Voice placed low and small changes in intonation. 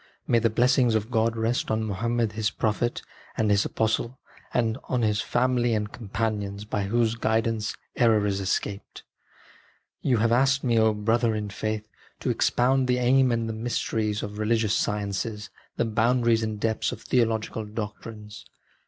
Yes: low, 110 Hz; narrow, 2.0 semitones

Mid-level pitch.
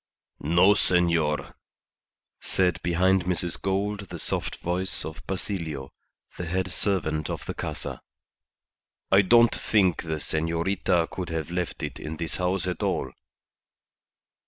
No: very low, 90 Hz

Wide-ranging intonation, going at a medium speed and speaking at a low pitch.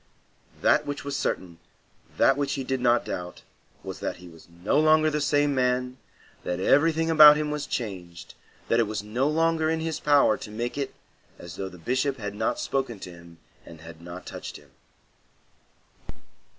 Yes: wide, 8.2 semitones; average, 180 wpm; low, 125 Hz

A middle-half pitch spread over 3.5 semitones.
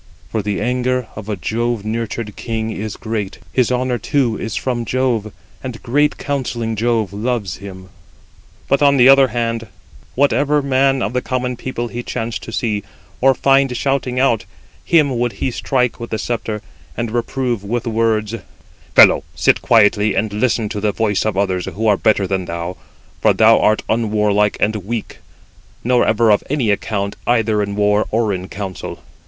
No: average, 3.2 semitones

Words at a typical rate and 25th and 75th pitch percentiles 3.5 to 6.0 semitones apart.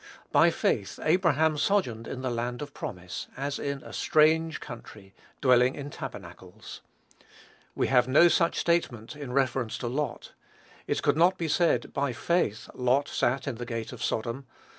Yes: average, 160 wpm; average, 4.3 semitones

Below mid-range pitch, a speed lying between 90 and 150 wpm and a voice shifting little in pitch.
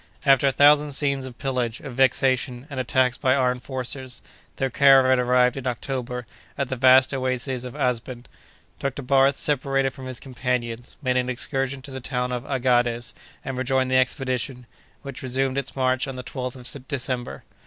No: low, 130 Hz; average, 175 wpm; narrow, 1.3 semitones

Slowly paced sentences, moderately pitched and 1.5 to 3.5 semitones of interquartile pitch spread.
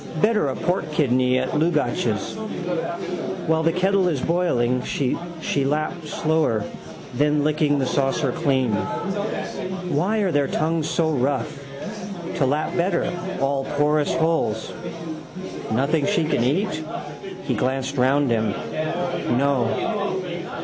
No: slow, 115 wpm; medium, 150 Hz; average, 4.2 semitones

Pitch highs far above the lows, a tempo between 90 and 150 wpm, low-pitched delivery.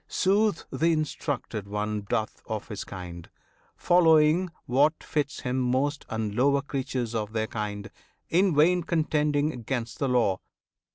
Yes: wide, 6.0 semitones; slow, 135 wpm; low, 130 Hz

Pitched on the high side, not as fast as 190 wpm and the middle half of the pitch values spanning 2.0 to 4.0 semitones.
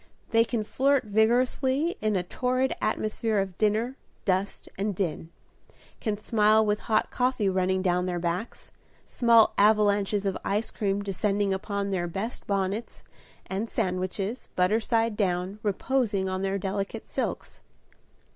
Yes: high, 205 Hz; slow, 135 wpm; average, 2.8 semitones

